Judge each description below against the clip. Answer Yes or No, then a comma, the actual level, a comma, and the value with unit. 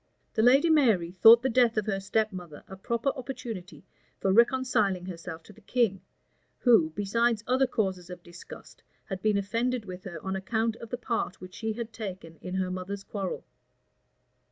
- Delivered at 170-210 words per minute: Yes, average, 180 wpm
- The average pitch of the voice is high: Yes, high, 210 Hz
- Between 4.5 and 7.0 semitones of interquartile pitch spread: No, average, 4.1 semitones